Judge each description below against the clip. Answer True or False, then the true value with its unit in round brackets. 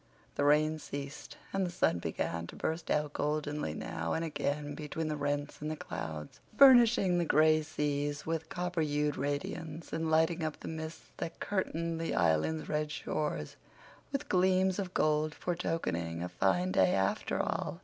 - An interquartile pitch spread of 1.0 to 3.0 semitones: True (2.5 semitones)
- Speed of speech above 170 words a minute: False (165 wpm)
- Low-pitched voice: False (155 Hz)